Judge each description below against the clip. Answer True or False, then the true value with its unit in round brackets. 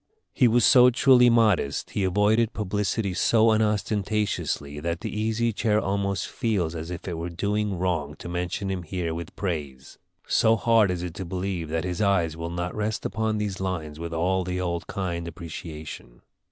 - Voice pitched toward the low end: True (95 Hz)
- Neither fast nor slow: True (180 wpm)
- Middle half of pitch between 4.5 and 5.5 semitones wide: False (3.9 semitones)